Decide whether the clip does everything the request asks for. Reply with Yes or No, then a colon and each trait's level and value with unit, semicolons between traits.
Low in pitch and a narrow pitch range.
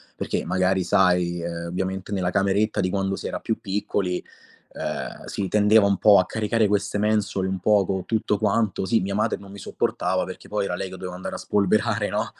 Yes: low, 100 Hz; narrow, 2.1 semitones